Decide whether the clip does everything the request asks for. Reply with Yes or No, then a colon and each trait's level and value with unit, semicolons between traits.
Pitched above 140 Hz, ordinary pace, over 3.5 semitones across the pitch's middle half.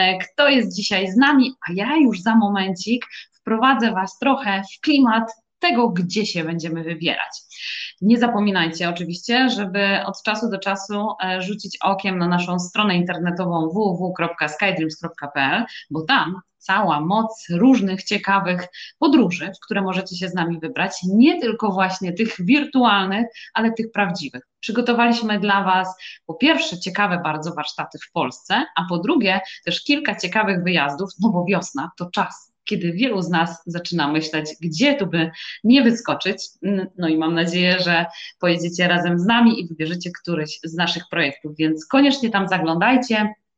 Yes: high, 190 Hz; average, 150 wpm; average, 4.5 semitones